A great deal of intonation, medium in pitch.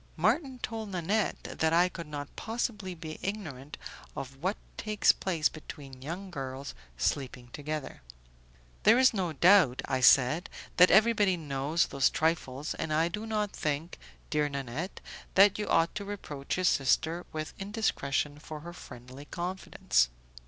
Yes: wide, 5.7 semitones; medium, 165 Hz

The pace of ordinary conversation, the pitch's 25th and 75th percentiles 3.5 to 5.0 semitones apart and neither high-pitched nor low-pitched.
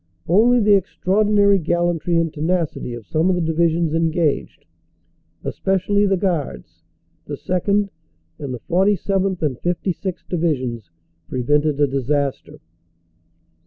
No: slow, 115 wpm; average, 4.4 semitones; medium, 170 Hz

